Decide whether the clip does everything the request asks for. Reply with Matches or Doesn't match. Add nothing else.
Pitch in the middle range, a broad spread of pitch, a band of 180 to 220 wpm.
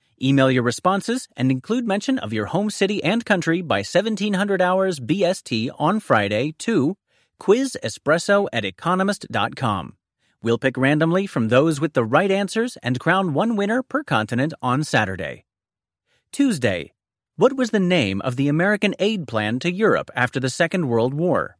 Doesn't match